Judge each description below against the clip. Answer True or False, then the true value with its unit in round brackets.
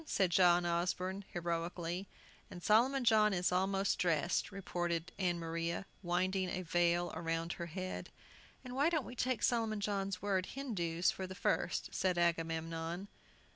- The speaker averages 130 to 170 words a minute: True (140 wpm)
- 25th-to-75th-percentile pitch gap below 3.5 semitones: True (2.6 semitones)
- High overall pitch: False (180 Hz)